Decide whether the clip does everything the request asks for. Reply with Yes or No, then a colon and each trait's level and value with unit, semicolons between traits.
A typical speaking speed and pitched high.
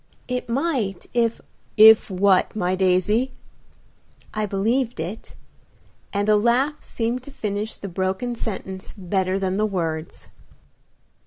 No: slow, 130 wpm; high, 210 Hz